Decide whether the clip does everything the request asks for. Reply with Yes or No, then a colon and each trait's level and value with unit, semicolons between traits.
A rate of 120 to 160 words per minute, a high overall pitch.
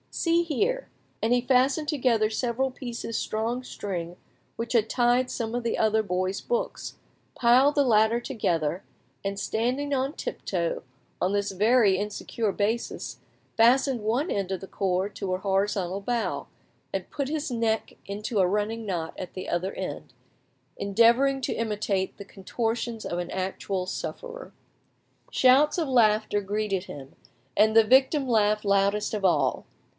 Yes: average, 150 wpm; high, 220 Hz